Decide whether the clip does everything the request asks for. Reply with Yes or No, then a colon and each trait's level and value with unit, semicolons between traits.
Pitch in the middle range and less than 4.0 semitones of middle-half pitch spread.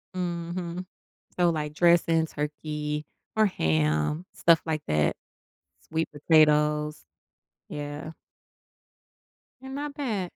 Yes: medium, 160 Hz; narrow, 2.6 semitones